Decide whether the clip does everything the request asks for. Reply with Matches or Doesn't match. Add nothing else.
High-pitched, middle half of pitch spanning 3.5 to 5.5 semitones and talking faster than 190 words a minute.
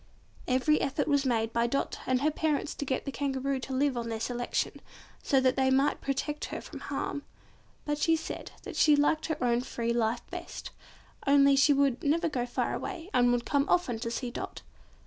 Doesn't match